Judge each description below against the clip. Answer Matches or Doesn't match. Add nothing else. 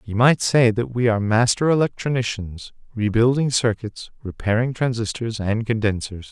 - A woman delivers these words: Doesn't match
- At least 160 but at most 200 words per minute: Doesn't match